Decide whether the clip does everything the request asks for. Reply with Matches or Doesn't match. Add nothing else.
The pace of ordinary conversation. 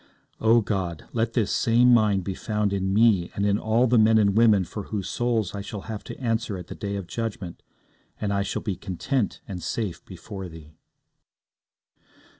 Matches